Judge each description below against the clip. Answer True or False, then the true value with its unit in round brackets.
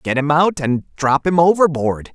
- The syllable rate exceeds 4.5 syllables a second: False (4.3 syllables/s)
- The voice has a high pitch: False (150 Hz)